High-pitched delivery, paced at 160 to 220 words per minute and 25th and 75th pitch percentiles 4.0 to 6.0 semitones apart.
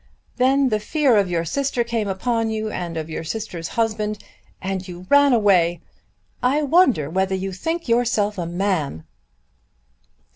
No: high, 210 Hz; average, 150 wpm; average, 5.2 semitones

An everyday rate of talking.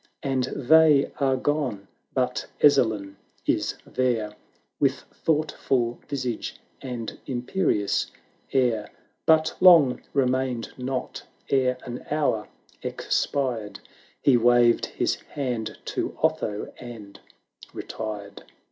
No: slow, 100 wpm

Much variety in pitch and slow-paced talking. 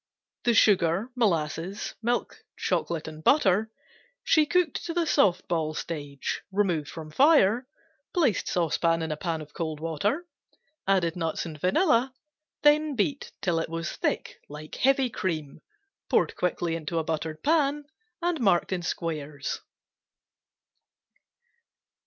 Yes: wide, 7.7 semitones; slow, 130 wpm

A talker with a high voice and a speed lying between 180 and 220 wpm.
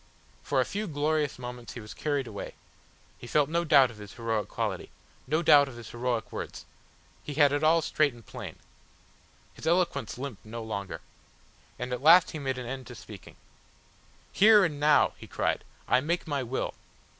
No: low, 135 Hz; average, 185 wpm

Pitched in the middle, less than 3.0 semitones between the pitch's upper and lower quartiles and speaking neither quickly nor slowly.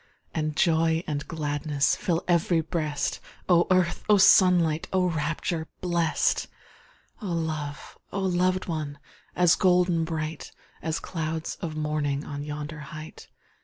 No: medium, 160 Hz; narrow, 2.5 semitones; slow, 130 wpm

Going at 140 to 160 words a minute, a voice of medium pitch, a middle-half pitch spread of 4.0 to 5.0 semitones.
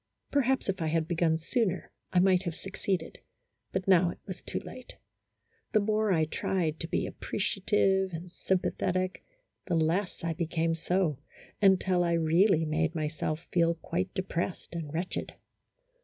No: average, 155 wpm; medium, 175 Hz; average, 2.7 semitones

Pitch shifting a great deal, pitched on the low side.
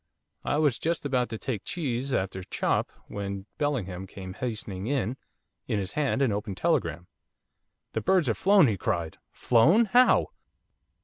Yes: wide, 6.9 semitones; low, 115 Hz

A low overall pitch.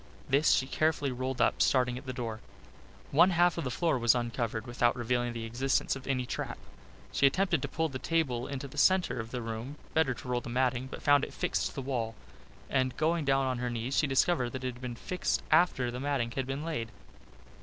Yes: low, 130 Hz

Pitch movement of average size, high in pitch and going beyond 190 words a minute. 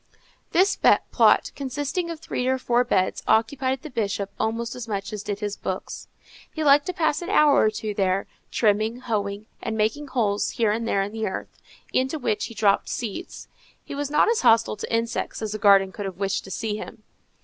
Yes: average, 4.4 semitones; high, 225 Hz; fast, 205 wpm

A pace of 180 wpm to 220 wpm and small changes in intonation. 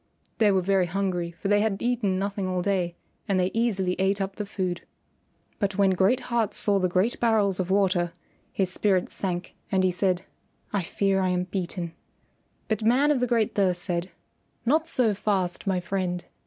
Yes: average, 185 wpm; narrow, 2.2 semitones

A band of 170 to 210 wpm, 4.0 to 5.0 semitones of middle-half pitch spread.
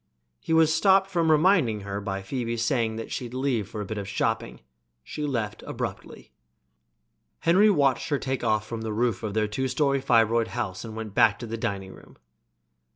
Yes: average, 185 wpm; average, 4.5 semitones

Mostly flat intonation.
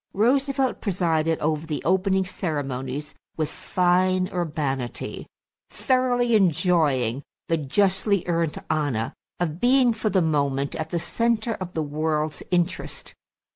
No: average, 4.5 semitones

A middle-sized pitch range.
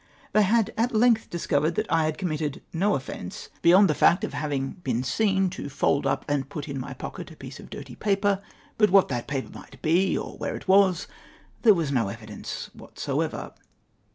No: wide, 6.2 semitones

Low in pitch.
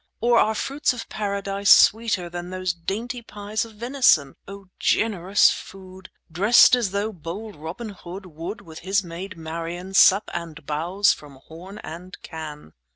No: high, 190 Hz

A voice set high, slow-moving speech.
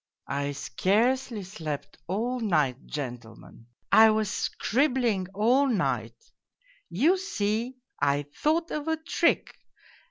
Yes: high, 210 Hz; slow, 115 wpm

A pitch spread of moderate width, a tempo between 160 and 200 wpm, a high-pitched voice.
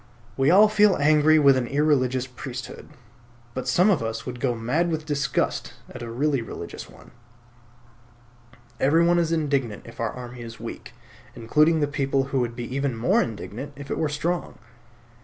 No: average, 4.0 semitones; average, 170 wpm; low, 135 Hz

